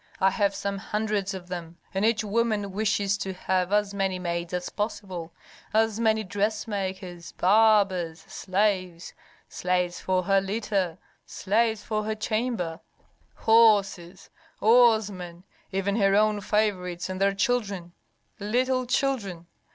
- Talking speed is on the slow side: Yes, slow, 125 wpm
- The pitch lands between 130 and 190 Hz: No, high, 200 Hz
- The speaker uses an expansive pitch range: No, average, 2.8 semitones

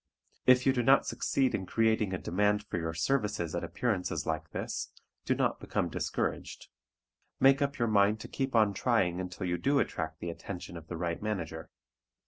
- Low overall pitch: Yes, low, 105 Hz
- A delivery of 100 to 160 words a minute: No, average, 185 wpm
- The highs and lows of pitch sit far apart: Yes, wide, 5.9 semitones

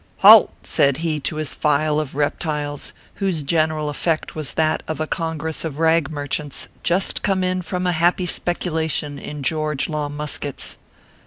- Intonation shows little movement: Yes, narrow, 2.0 semitones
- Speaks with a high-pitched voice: No, medium, 155 Hz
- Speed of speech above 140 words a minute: Yes, average, 175 wpm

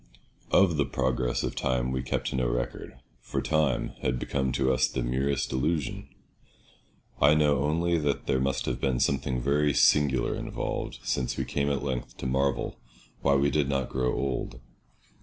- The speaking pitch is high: No, very low, 65 Hz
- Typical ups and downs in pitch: No, narrow, 2.1 semitones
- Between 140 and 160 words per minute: No, average, 170 wpm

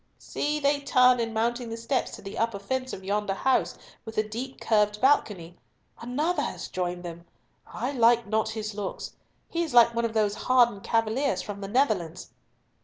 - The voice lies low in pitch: No, high, 225 Hz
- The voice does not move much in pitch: No, average, 3.7 semitones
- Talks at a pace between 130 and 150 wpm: No, average, 180 wpm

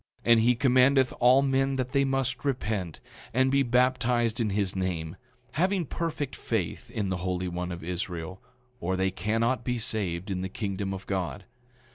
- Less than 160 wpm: No, average, 175 wpm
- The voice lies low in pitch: Yes, low, 110 Hz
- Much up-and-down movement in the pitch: Yes, wide, 5.7 semitones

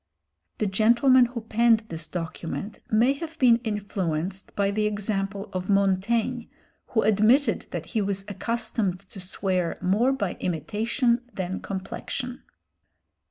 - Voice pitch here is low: No, high, 210 Hz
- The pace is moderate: No, slow, 125 wpm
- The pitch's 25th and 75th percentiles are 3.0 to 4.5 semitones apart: Yes, average, 3.6 semitones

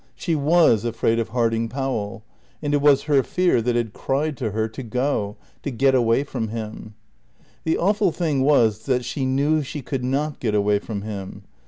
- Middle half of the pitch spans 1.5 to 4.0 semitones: No, average, 4.5 semitones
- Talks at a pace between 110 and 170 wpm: No, average, 190 wpm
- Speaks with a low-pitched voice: Yes, low, 125 Hz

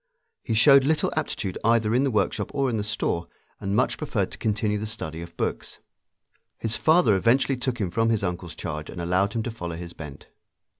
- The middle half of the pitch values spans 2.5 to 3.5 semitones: No, average, 5.1 semitones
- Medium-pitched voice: No, low, 105 Hz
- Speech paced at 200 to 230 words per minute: Yes, fast, 205 wpm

